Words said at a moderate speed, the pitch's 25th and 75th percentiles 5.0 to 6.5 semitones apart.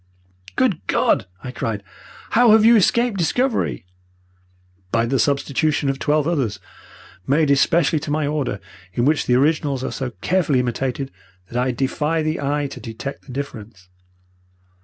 No: average, 150 wpm; average, 4.1 semitones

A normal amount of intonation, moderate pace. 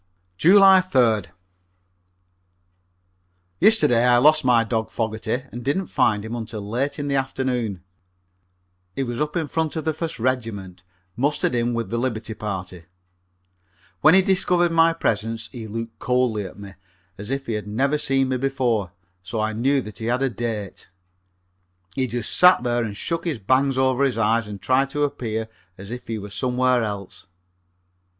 Yes: average, 3.9 semitones; average, 170 wpm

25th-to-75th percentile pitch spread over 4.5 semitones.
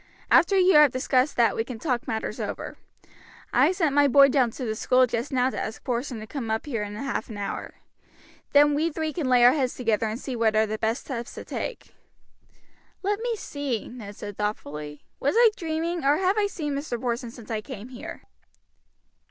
Yes: average, 4.9 semitones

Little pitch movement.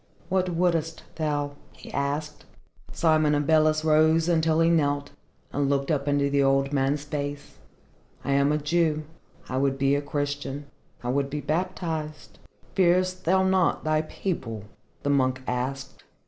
Yes: narrow, 2.3 semitones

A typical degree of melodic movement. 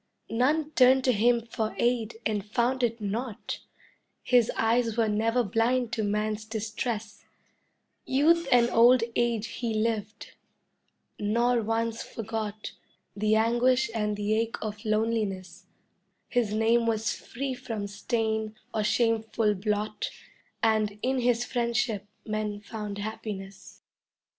No: narrow, 2.0 semitones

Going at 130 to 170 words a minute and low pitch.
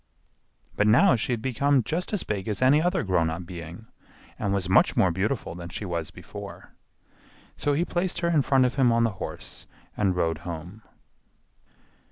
No: average, 185 wpm; low, 105 Hz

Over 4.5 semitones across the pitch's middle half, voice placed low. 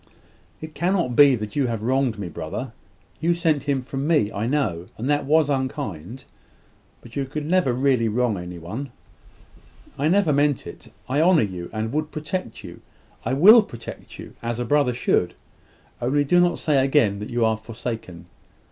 Yes: average, 4.9 semitones; low, 130 Hz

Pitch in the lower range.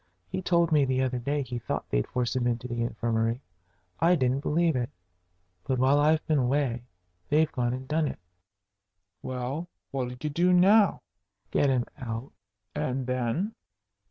Yes: low, 130 Hz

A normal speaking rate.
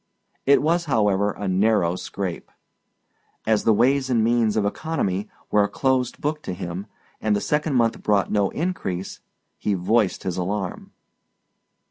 Yes: average, 150 wpm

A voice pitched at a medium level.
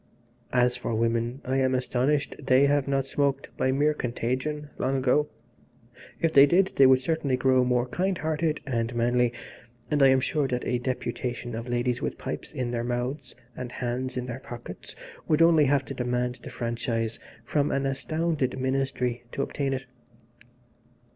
No: low, 130 Hz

